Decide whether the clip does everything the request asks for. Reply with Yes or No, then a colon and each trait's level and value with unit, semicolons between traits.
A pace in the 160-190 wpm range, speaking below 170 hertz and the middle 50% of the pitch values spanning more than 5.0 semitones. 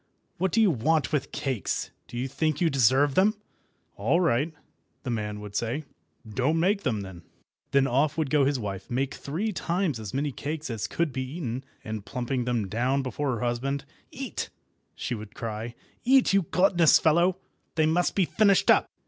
Yes: average, 180 wpm; medium, 140 Hz; wide, 5.4 semitones